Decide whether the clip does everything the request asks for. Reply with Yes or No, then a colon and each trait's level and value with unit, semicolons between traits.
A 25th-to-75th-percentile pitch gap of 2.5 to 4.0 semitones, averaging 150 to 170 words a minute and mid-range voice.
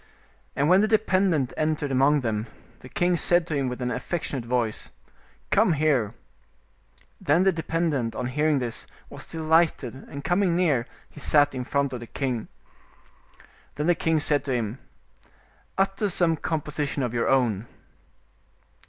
No: average, 4.6 semitones; average, 155 wpm; medium, 145 Hz